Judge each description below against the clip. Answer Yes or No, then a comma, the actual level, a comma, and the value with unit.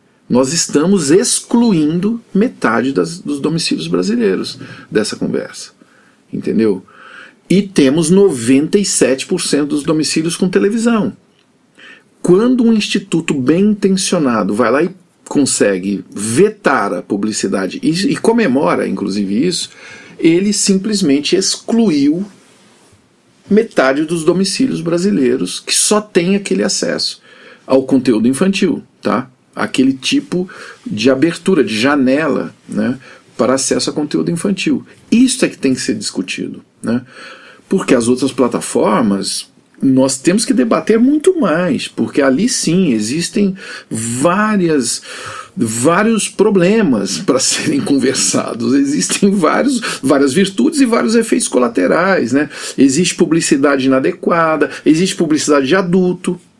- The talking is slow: Yes, slow, 115 wpm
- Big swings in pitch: Yes, wide, 6.3 semitones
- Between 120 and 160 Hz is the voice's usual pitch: No, medium, 185 Hz